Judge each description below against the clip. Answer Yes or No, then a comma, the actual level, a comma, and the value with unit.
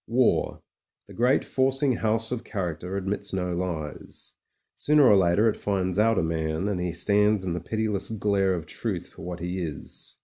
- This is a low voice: Yes, very low, 95 Hz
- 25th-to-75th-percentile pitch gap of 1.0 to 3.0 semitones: No, average, 3.9 semitones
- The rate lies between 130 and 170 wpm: No, average, 180 wpm